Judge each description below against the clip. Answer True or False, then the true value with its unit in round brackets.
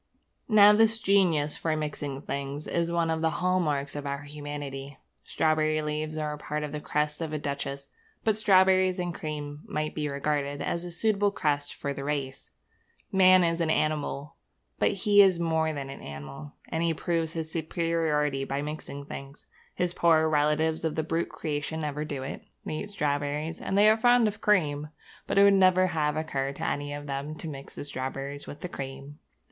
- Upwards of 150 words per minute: True (195 wpm)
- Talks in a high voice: False (155 Hz)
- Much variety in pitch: False (2.9 semitones)